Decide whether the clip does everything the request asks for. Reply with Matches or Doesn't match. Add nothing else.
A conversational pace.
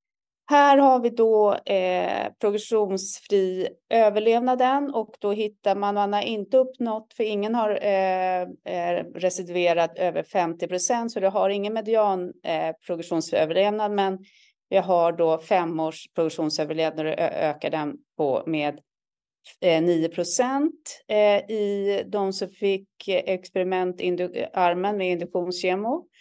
Doesn't match